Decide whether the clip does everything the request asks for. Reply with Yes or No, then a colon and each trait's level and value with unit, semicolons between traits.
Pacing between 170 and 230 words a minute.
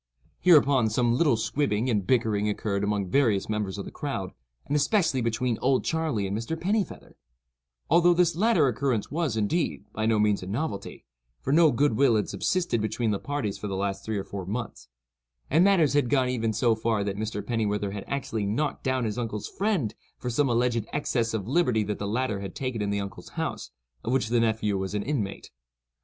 Yes: average, 200 wpm